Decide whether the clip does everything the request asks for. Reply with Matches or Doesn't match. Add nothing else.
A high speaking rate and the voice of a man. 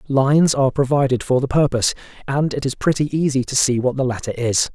Matches